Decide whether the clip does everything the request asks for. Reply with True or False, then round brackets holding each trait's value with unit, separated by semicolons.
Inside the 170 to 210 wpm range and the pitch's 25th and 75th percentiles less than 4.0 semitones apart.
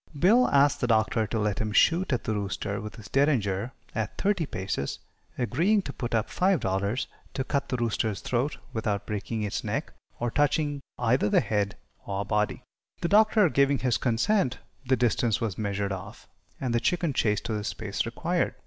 False (180 wpm; 5.2 semitones)